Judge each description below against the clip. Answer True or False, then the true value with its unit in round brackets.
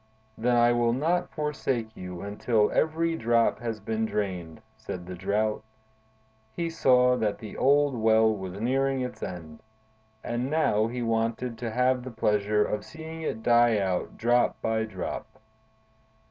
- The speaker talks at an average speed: True (150 wpm)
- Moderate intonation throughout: True (3.1 semitones)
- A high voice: False (115 Hz)